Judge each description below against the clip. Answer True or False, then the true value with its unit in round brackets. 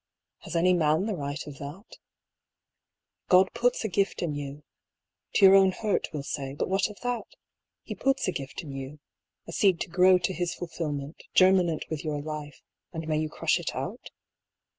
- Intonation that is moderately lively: True (4.2 semitones)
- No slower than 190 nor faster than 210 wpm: True (195 wpm)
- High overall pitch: False (170 Hz)